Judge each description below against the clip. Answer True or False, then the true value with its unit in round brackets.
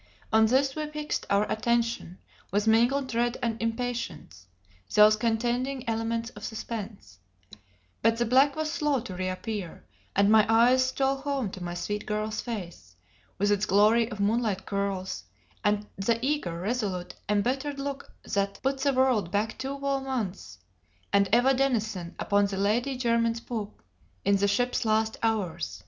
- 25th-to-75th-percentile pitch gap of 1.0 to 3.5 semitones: False (3.9 semitones)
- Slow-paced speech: False (155 wpm)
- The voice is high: True (225 Hz)